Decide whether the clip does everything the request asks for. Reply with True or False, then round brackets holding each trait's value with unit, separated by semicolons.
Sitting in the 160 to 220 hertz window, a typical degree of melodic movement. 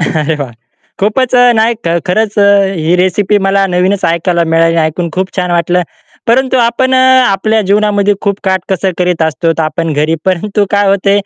True (190 Hz; 3.5 semitones)